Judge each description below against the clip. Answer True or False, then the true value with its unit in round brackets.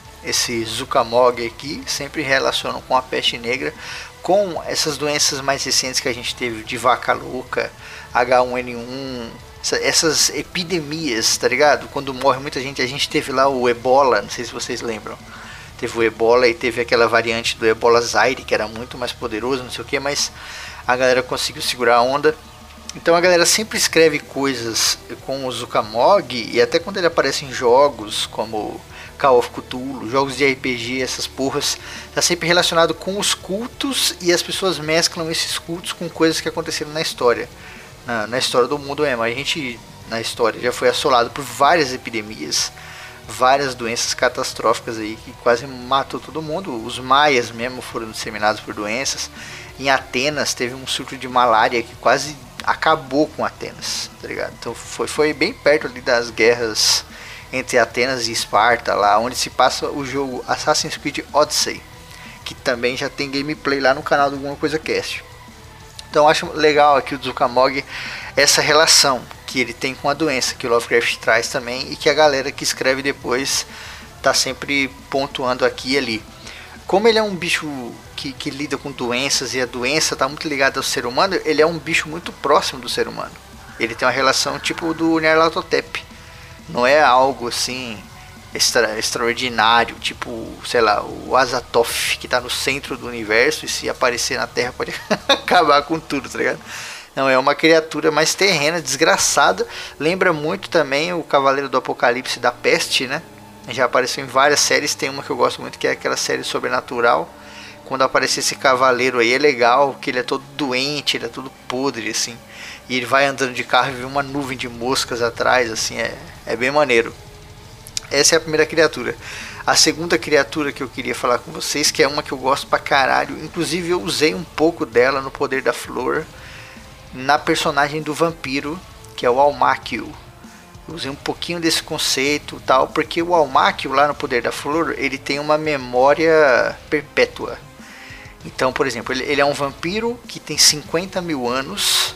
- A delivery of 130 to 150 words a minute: False (180 wpm)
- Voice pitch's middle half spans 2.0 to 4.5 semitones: True (4.0 semitones)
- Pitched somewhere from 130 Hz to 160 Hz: True (140 Hz)